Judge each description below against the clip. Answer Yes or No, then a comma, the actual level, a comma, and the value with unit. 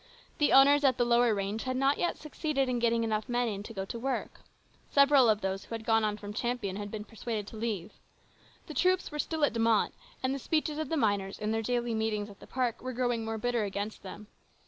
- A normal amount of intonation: Yes, average, 3.5 semitones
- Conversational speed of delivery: No, fast, 240 wpm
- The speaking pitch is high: Yes, high, 230 Hz